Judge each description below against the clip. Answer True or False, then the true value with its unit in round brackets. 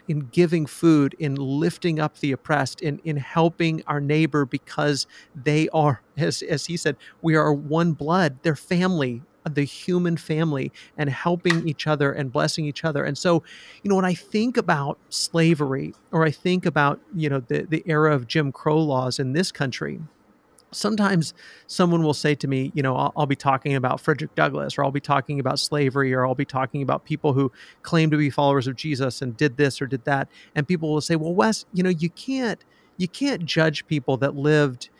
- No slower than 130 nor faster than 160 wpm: False (200 wpm)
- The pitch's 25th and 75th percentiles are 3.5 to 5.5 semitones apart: False (2.9 semitones)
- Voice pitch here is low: False (150 Hz)